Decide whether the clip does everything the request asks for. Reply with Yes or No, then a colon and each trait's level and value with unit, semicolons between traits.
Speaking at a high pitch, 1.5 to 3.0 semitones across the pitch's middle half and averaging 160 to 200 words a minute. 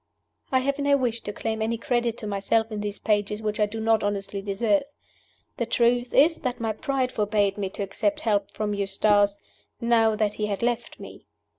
Yes: high, 220 Hz; narrow, 2.5 semitones; average, 195 wpm